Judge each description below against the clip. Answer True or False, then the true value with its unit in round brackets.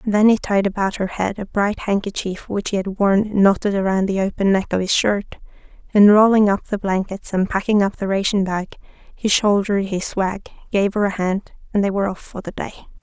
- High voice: True (200 Hz)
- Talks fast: True (215 wpm)